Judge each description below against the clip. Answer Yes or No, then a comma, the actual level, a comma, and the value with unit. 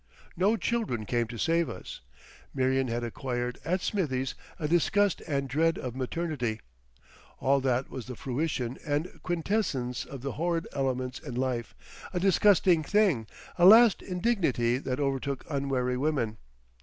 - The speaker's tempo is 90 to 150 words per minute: Yes, average, 145 wpm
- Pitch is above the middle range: No, medium, 140 Hz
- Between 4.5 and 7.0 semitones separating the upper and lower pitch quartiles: Yes, average, 5.2 semitones